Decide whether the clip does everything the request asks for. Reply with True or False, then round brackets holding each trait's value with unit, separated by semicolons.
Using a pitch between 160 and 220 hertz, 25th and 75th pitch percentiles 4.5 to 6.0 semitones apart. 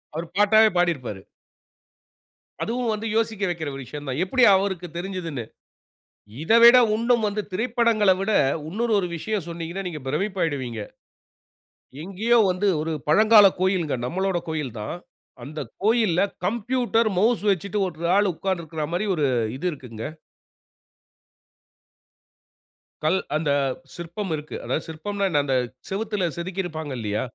True (185 Hz; 5.2 semitones)